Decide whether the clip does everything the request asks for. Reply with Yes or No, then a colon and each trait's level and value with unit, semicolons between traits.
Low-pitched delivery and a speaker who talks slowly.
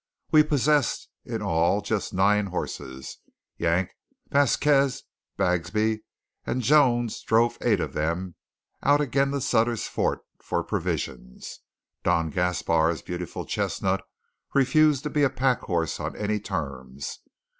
Yes: low, 105 Hz; slow, 125 wpm